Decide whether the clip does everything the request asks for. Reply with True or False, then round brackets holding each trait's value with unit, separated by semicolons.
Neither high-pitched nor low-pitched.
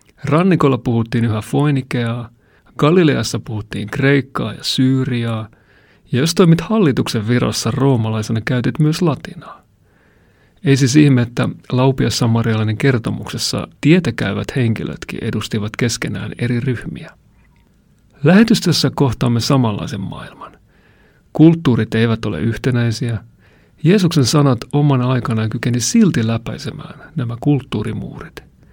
False (125 Hz)